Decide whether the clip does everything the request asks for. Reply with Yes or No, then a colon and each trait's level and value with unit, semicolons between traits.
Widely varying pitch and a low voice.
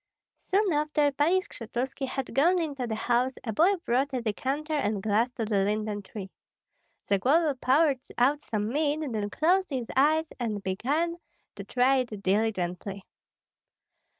No: wide, 5.9 semitones; very high, 255 Hz